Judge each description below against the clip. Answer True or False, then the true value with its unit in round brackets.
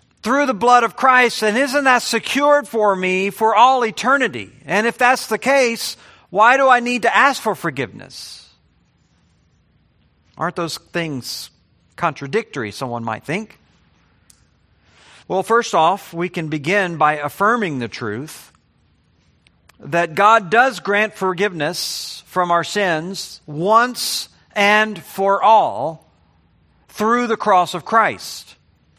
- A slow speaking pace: True (125 wpm)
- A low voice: False (195 Hz)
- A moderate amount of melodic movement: False (7.2 semitones)